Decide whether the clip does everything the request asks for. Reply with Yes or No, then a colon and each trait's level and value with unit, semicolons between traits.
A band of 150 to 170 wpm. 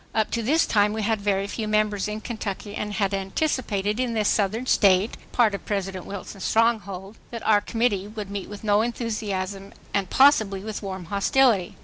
No: average, 190 wpm